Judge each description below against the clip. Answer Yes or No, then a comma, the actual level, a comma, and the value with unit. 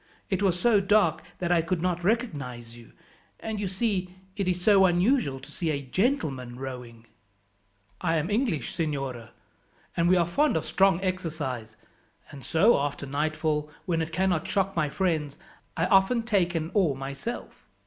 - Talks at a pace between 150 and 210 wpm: Yes, average, 165 wpm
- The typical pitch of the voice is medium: Yes, medium, 170 Hz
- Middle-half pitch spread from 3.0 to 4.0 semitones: No, average, 5.2 semitones